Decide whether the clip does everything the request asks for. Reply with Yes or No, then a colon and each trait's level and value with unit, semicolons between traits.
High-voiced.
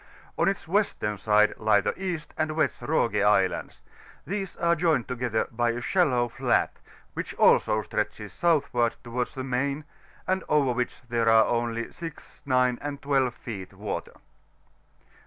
No: low, 125 Hz